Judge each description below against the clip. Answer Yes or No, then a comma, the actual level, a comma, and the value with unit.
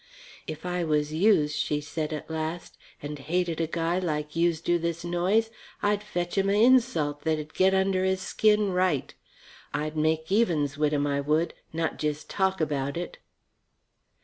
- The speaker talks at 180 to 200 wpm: No, average, 170 wpm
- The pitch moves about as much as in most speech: Yes, average, 3.6 semitones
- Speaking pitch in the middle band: Yes, medium, 165 Hz